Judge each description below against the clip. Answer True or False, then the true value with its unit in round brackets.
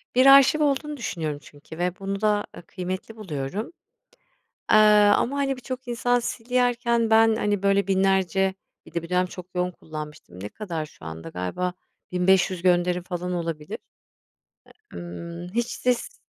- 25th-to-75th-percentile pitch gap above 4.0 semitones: True (5.2 semitones)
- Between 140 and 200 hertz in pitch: True (190 Hz)